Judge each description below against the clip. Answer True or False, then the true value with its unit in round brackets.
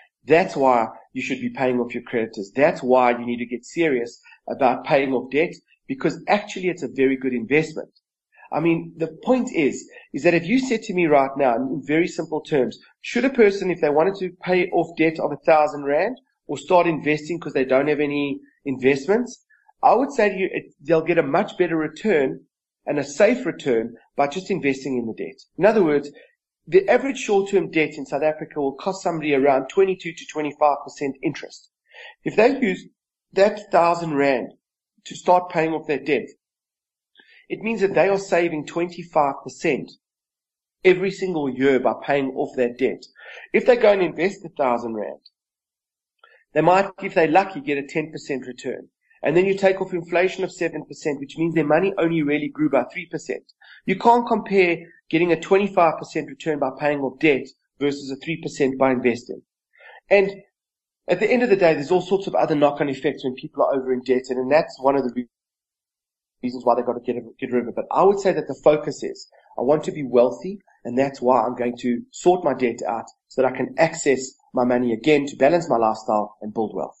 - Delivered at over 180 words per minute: True (200 wpm)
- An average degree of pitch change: False (5.7 semitones)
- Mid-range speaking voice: True (155 Hz)